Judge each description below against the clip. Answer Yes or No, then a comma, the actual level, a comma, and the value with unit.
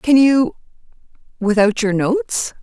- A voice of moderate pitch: No, high, 230 Hz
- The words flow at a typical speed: No, slow, 90 wpm